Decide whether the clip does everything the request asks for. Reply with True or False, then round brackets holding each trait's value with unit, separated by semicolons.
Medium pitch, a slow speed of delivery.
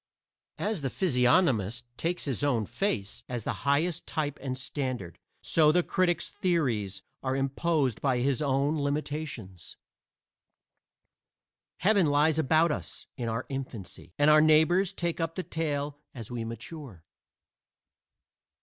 True (145 Hz; 130 wpm)